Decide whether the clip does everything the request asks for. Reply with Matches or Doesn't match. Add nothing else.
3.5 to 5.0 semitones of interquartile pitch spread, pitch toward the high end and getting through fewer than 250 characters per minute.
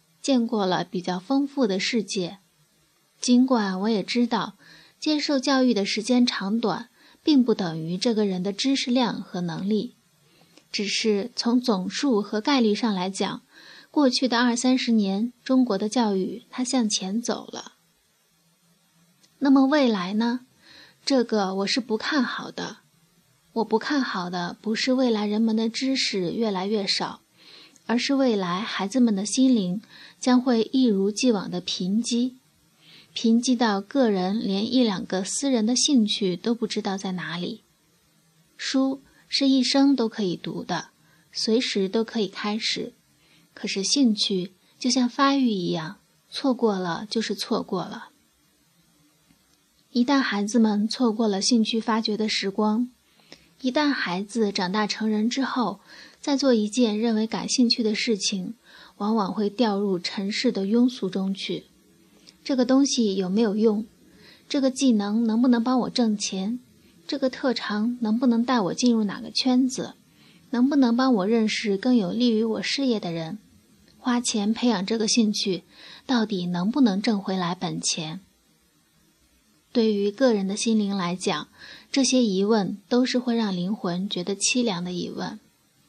Matches